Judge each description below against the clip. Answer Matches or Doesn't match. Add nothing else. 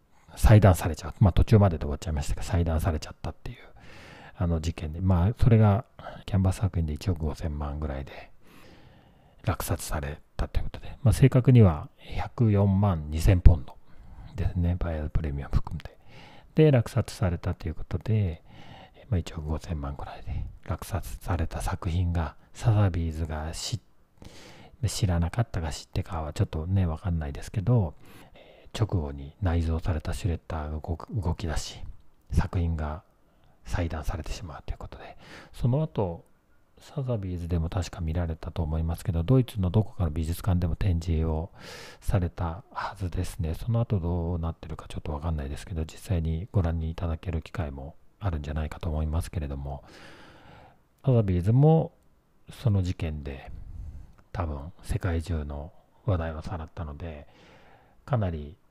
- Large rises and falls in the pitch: Doesn't match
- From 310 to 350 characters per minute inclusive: Matches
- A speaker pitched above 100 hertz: Doesn't match